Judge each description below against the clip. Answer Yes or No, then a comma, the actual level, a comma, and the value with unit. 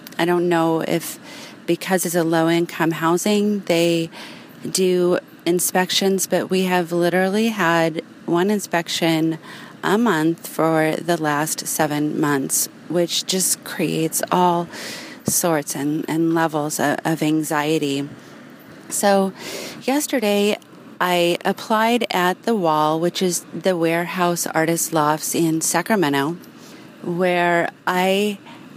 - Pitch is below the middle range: No, medium, 175 Hz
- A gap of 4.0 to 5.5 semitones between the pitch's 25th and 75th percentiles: No, narrow, 2.5 semitones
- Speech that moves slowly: Yes, slow, 115 wpm